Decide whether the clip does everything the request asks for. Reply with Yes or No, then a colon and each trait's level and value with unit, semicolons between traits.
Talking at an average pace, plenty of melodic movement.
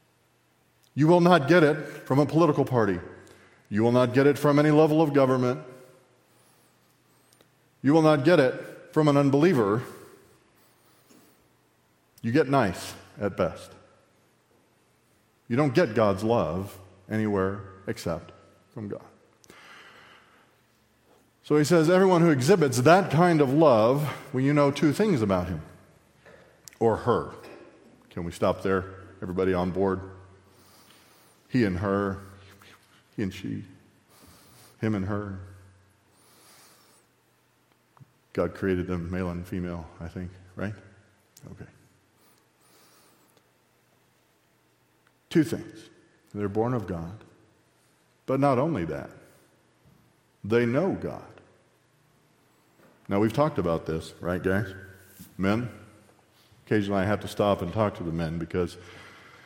No: slow, 120 wpm; wide, 6.1 semitones